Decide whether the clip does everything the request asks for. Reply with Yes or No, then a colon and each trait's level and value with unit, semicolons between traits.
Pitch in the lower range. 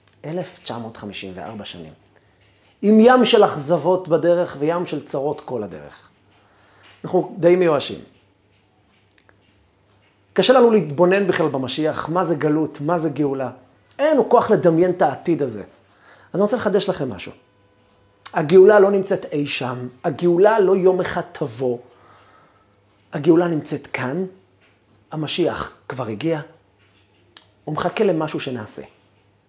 No: medium, 145 Hz